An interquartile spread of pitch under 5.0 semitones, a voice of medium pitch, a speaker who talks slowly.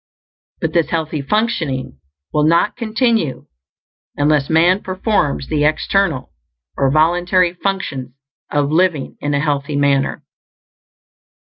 Yes: average, 4.5 semitones; medium, 155 Hz; slow, 110 wpm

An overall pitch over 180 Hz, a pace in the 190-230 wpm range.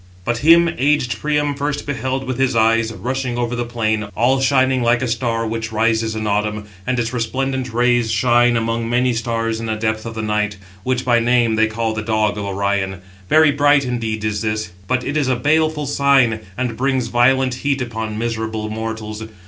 No: low, 120 Hz; average, 195 wpm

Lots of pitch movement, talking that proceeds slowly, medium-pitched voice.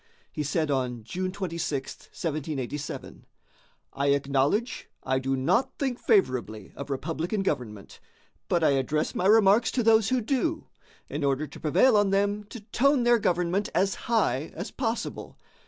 No: wide, 7.6 semitones; average, 150 wpm; medium, 170 Hz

